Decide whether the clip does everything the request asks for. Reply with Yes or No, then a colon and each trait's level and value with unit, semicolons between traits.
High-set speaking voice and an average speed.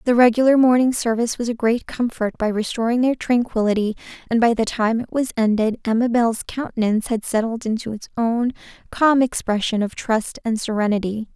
Yes: high, 230 Hz; average, 170 wpm